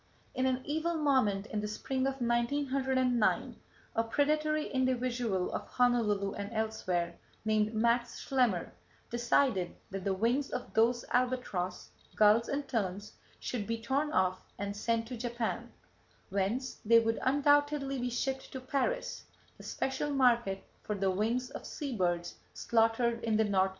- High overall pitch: Yes, high, 235 Hz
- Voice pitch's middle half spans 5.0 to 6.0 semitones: No, average, 3.9 semitones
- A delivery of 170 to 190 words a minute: No, average, 150 wpm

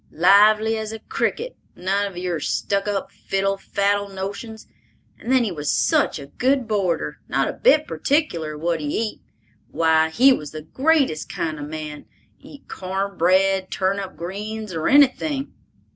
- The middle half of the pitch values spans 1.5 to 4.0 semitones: No, average, 4.7 semitones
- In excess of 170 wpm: No, average, 155 wpm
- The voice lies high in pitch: Yes, high, 195 Hz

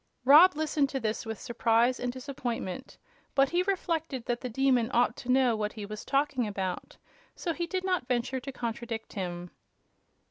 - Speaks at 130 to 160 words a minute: No, average, 175 wpm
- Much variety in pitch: No, average, 3.7 semitones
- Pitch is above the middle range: Yes, very high, 250 Hz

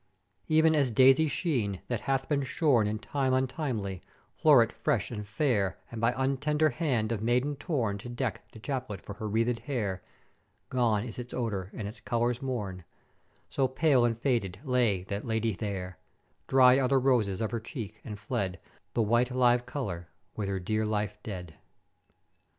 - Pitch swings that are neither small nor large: Yes, average, 4.1 semitones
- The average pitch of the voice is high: No, low, 120 Hz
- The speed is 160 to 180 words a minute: Yes, average, 170 wpm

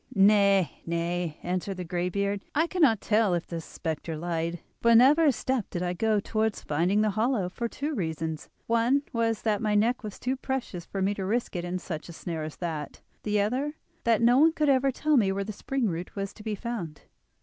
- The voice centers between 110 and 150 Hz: No, high, 205 Hz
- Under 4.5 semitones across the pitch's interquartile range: No, average, 5.0 semitones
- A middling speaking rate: No, fast, 210 wpm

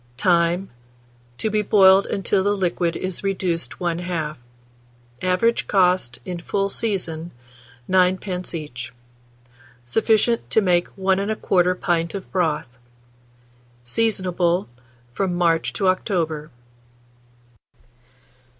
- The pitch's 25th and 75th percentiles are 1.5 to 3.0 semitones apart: Yes, narrow, 2.5 semitones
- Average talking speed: No, slow, 100 wpm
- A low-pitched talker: No, medium, 180 Hz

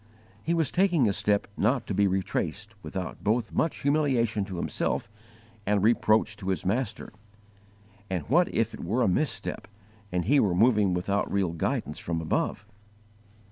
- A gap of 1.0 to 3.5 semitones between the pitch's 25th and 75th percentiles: No, average, 4.7 semitones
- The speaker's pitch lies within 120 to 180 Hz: No, low, 105 Hz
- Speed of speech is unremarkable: Yes, average, 160 wpm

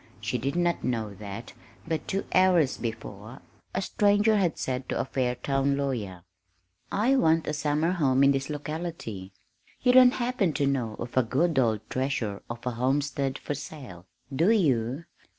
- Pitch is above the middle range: No, medium, 140 Hz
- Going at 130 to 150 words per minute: No, average, 165 wpm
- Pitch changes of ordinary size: No, wide, 5.9 semitones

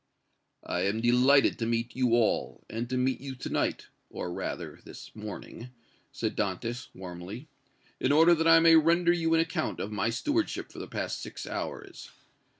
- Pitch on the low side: Yes, low, 125 Hz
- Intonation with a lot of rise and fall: Yes, wide, 6.2 semitones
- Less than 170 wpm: No, average, 175 wpm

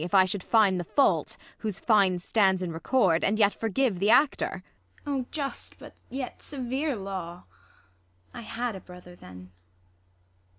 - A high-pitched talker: Yes, high, 200 Hz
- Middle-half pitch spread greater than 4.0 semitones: Yes, wide, 5.4 semitones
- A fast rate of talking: No, average, 160 wpm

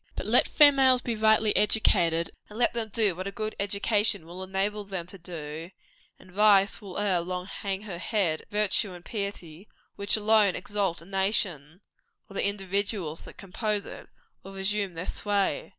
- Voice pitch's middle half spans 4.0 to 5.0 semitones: No, average, 2.7 semitones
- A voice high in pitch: Yes, high, 200 Hz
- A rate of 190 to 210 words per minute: No, average, 175 wpm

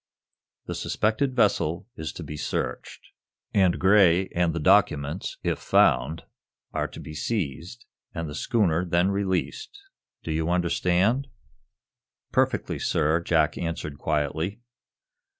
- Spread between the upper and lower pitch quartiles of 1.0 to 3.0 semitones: No, average, 3.9 semitones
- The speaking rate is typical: No, slow, 120 wpm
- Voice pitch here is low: Yes, very low, 85 Hz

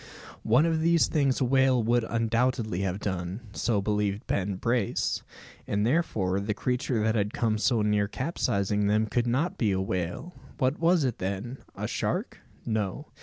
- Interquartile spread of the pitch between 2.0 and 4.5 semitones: Yes, average, 4.2 semitones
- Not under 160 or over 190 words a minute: Yes, average, 170 wpm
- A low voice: Yes, low, 110 Hz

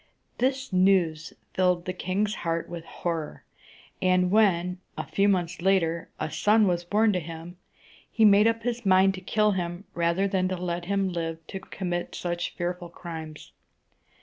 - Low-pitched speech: No, medium, 180 Hz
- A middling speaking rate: Yes, average, 160 wpm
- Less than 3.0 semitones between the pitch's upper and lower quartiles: Yes, narrow, 2.4 semitones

